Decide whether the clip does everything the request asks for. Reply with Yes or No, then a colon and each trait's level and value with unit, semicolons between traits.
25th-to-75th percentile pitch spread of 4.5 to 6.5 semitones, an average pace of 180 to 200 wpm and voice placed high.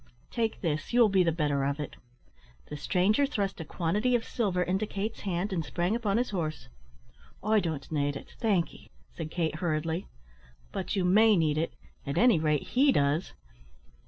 No: average, 5.3 semitones; average, 185 wpm; medium, 180 Hz